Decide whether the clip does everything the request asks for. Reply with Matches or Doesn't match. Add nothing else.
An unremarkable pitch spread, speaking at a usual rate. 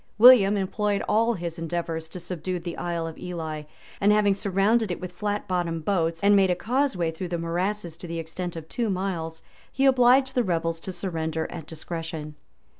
Matches